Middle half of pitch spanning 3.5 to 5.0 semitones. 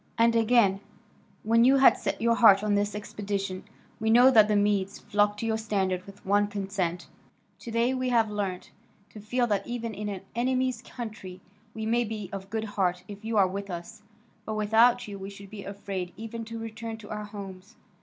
No: narrow, 2.4 semitones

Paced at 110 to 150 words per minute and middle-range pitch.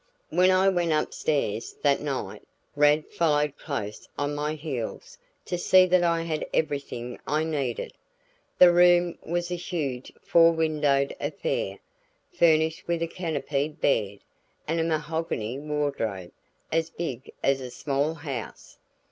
Yes: slow, 135 wpm; medium, 155 Hz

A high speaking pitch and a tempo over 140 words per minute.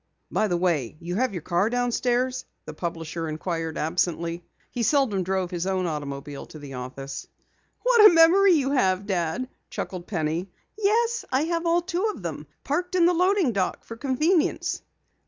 Yes: high, 195 Hz; average, 170 wpm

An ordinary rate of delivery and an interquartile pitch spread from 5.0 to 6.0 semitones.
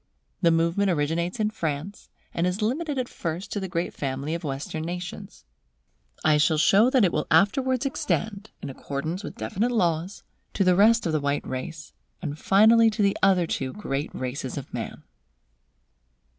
Yes: average, 170 wpm; wide, 5.5 semitones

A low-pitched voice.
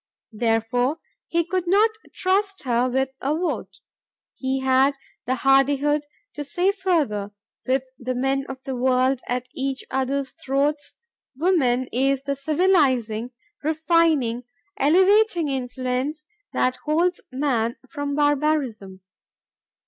No: very high, 275 Hz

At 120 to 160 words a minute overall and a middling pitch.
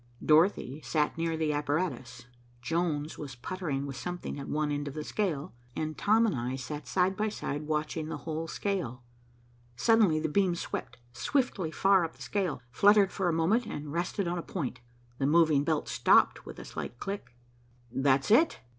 No: average, 180 wpm; medium, 160 Hz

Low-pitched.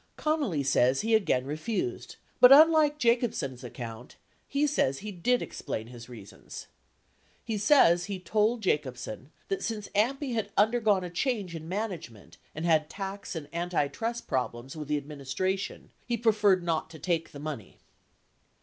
No: medium, 180 Hz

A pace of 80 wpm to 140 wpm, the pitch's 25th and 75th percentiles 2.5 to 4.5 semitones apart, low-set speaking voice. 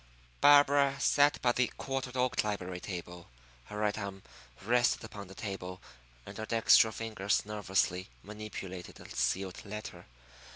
Yes: slow, 135 wpm; average, 4.1 semitones; low, 105 Hz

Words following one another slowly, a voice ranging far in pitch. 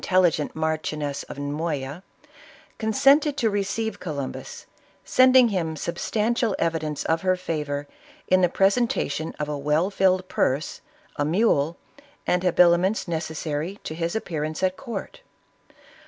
No: slow, 125 wpm; average, 4.4 semitones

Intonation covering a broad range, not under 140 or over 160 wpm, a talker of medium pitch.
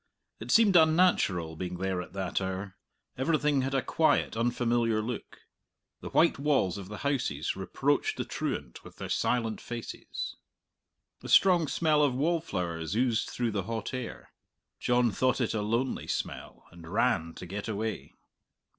No: wide, 6.1 semitones; average, 155 wpm; low, 115 Hz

